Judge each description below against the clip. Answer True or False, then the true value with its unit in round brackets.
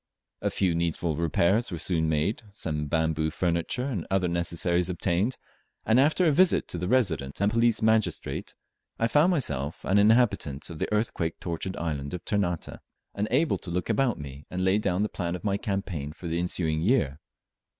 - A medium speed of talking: True (180 wpm)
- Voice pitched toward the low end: True (90 Hz)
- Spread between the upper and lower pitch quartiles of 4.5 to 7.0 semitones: True (4.9 semitones)